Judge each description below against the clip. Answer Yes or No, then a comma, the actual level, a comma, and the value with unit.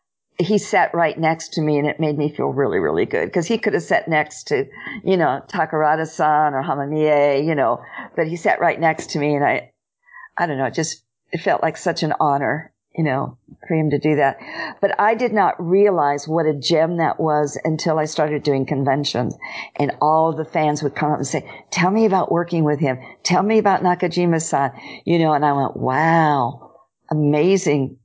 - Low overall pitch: No, medium, 155 Hz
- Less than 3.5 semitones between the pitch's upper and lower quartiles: Yes, average, 2.9 semitones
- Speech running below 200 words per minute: No, fast, 205 wpm